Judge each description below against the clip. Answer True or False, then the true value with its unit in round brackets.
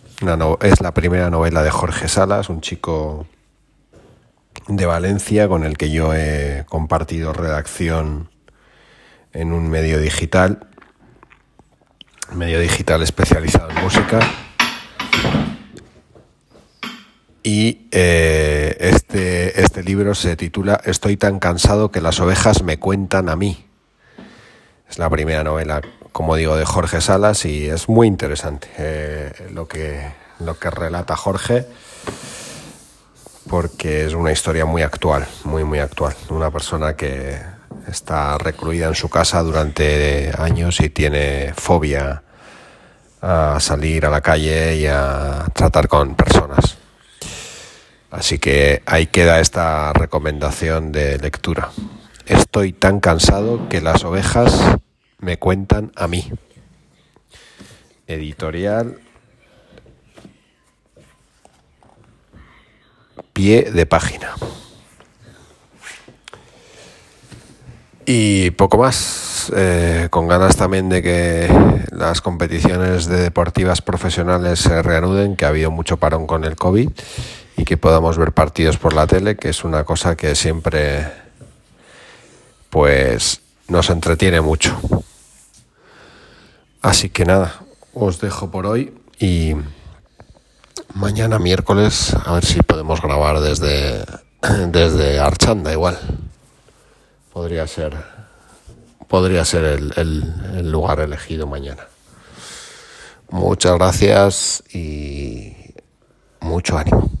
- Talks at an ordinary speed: False (110 wpm)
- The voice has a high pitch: False (85 Hz)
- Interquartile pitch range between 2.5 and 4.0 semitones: True (3.4 semitones)